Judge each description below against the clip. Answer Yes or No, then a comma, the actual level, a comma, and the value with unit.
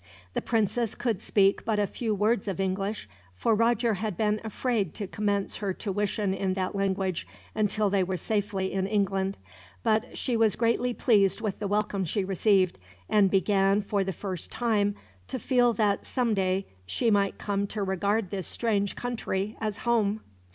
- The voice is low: No, high, 205 Hz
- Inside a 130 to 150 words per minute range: No, average, 170 wpm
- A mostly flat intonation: Yes, narrow, 2.2 semitones